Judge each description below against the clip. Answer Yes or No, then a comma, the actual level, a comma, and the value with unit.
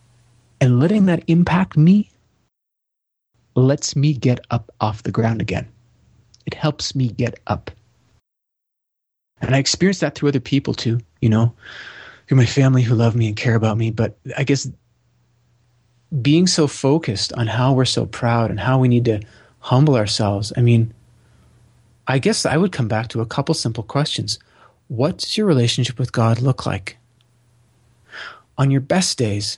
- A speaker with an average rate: Yes, average, 160 wpm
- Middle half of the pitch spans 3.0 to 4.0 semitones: Yes, average, 3.3 semitones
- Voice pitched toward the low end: Yes, low, 120 Hz